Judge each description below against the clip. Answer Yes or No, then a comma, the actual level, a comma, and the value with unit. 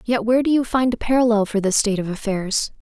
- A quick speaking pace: Yes, fast, 255 wpm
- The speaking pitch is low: No, high, 225 Hz